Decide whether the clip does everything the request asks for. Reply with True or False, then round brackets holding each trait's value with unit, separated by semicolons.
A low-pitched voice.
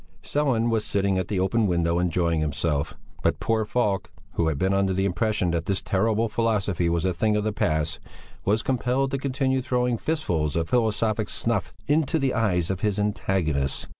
True (100 Hz)